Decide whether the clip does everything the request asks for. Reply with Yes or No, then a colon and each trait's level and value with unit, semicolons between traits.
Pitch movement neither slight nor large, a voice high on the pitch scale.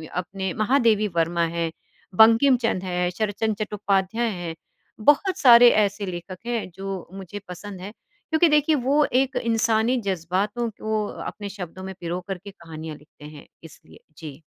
Yes: average, 4.2 semitones; high, 200 Hz